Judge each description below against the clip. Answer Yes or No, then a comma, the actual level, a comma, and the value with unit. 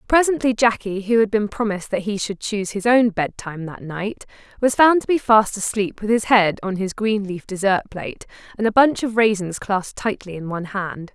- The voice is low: No, high, 210 Hz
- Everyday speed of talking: No, fast, 215 wpm